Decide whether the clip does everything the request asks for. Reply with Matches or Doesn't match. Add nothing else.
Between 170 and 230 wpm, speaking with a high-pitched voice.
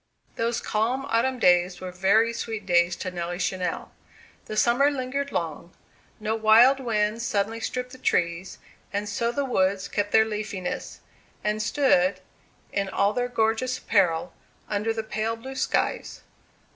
Doesn't match